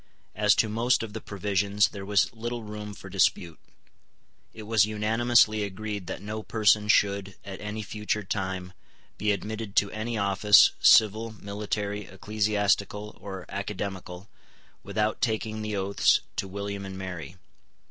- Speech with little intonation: Yes, narrow, 1.6 semitones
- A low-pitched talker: Yes, low, 105 Hz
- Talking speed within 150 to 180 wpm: No, average, 140 wpm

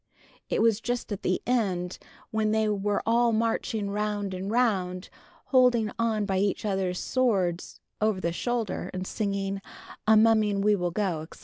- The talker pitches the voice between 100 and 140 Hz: No, high, 210 Hz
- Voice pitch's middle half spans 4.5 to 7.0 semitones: No, average, 2.9 semitones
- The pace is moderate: Yes, average, 165 wpm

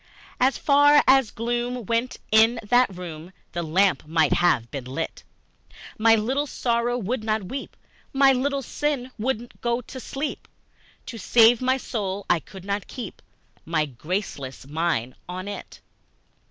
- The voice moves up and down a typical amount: No, wide, 6.3 semitones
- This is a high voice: Yes, high, 225 Hz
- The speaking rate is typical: Yes, average, 145 wpm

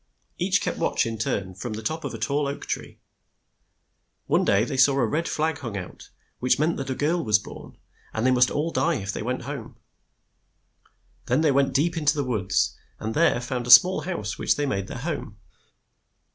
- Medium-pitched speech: No, low, 130 Hz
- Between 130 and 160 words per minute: No, fast, 205 wpm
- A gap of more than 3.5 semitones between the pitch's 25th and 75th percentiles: Yes, average, 5.2 semitones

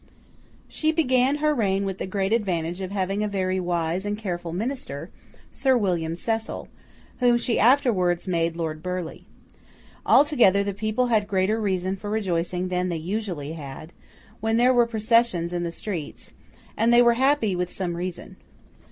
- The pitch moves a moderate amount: Yes, average, 4.6 semitones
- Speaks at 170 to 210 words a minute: No, average, 160 wpm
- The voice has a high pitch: Yes, high, 195 Hz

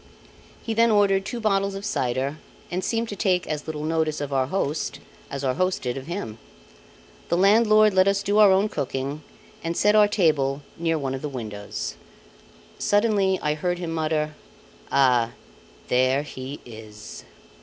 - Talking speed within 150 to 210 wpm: Yes, average, 165 wpm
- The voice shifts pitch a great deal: Yes, wide, 6.5 semitones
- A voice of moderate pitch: Yes, medium, 160 Hz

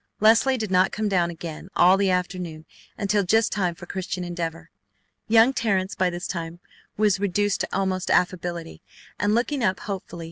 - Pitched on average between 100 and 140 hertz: No, medium, 185 Hz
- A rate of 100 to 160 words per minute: No, average, 170 wpm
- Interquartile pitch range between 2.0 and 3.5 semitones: Yes, average, 2.8 semitones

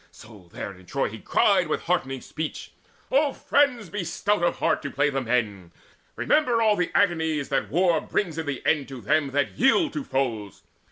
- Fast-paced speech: No, average, 190 wpm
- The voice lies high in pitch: No, medium, 155 Hz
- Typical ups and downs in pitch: No, wide, 7.8 semitones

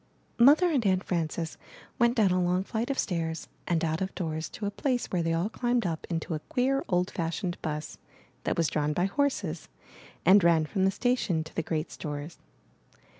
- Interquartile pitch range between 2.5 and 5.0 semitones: No, wide, 5.4 semitones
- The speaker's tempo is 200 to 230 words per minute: Yes, fast, 205 wpm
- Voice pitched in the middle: Yes, medium, 180 Hz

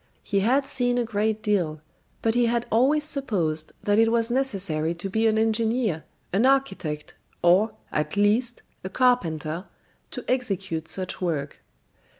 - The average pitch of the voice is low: No, high, 215 Hz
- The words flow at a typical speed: Yes, average, 150 wpm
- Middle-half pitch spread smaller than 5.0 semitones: No, wide, 5.6 semitones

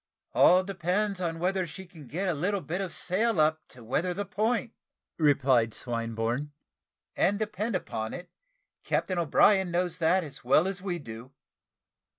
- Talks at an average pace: Yes, average, 160 wpm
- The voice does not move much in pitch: No, average, 5.0 semitones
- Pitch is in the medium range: Yes, medium, 175 Hz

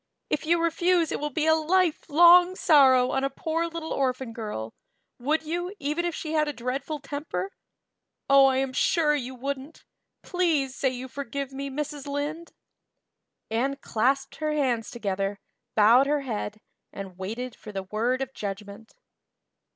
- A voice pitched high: Yes, very high, 275 Hz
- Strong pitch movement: No, average, 4.2 semitones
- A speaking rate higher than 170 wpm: No, average, 160 wpm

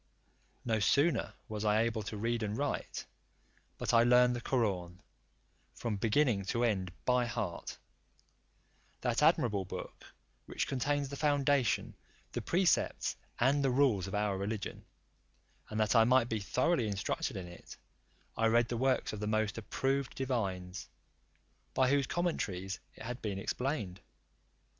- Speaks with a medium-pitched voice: No, low, 115 Hz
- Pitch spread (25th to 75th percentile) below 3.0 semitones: No, average, 4.2 semitones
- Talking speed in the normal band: Yes, average, 145 wpm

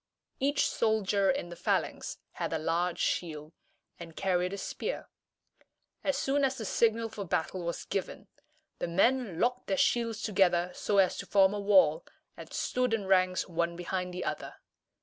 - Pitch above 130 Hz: Yes, high, 190 Hz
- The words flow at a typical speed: Yes, average, 170 wpm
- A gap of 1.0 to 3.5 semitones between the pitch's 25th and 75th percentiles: No, average, 4.4 semitones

